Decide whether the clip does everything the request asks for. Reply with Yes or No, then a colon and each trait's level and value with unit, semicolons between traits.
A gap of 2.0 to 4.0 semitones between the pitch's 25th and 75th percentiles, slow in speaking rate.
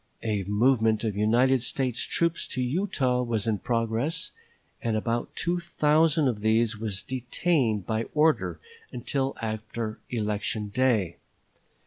Yes: average, 3.5 semitones; slow, 125 wpm